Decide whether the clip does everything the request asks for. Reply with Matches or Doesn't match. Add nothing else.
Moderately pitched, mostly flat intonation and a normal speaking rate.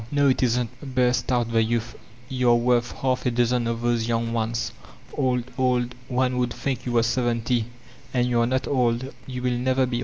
Doesn't match